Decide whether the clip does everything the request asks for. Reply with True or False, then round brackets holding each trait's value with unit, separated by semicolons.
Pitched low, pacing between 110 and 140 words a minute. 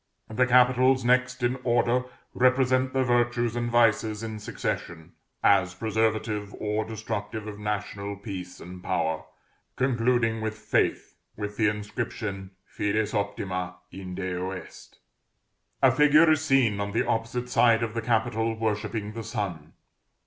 True (110 Hz; 135 wpm)